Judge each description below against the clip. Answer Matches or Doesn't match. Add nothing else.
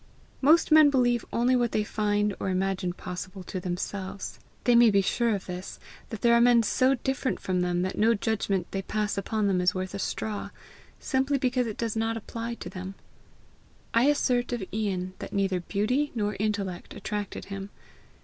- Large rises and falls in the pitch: Doesn't match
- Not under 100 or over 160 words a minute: Doesn't match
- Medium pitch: Doesn't match